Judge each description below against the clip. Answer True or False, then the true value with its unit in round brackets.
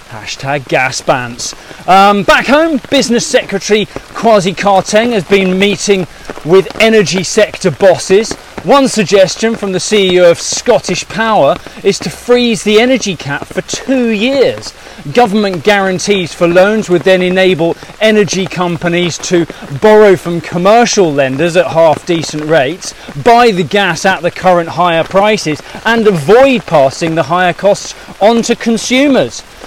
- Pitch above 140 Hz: True (190 Hz)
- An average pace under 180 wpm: True (140 wpm)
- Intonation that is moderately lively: True (3.8 semitones)